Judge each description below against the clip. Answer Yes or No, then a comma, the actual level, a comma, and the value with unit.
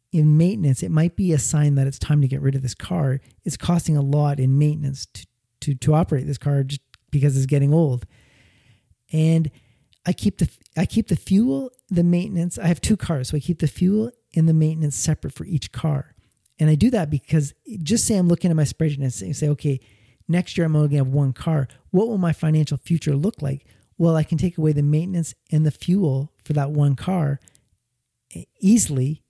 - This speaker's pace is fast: Yes, fast, 215 wpm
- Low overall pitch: No, medium, 150 Hz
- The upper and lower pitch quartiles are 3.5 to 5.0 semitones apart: Yes, average, 3.9 semitones